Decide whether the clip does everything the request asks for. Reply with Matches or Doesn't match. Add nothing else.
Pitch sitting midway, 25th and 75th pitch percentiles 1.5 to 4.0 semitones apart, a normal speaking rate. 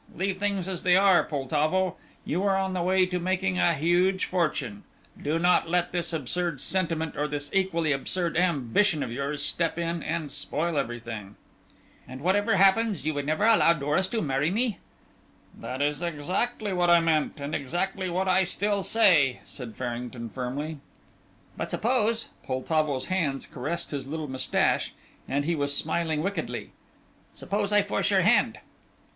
Doesn't match